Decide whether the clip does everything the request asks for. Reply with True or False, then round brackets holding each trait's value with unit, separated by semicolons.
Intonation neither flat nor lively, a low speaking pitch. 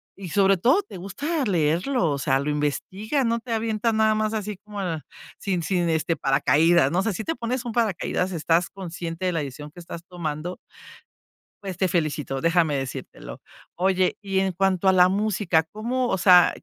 False (4.6 semitones; 185 Hz)